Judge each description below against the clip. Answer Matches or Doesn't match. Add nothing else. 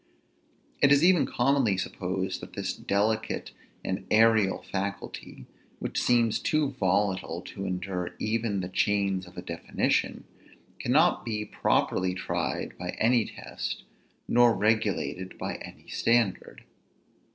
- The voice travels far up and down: Doesn't match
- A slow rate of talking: Matches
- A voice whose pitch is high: Doesn't match